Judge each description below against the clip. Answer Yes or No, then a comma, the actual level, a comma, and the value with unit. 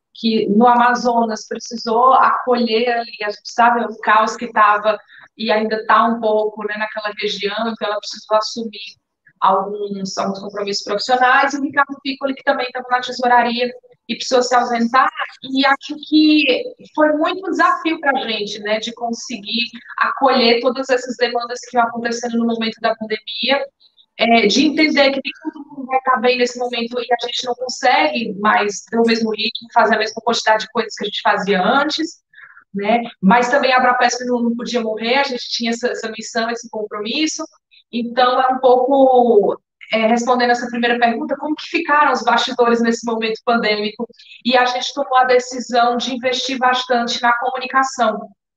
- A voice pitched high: Yes, high, 240 Hz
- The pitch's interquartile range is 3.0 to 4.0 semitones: No, narrow, 2.5 semitones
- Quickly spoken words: No, average, 175 wpm